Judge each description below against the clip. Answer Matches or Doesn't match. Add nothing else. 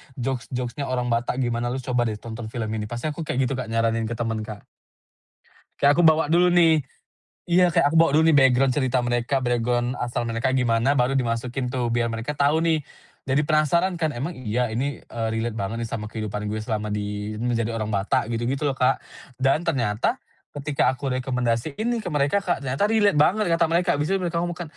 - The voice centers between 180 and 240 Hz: Doesn't match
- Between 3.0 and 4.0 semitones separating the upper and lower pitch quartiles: Doesn't match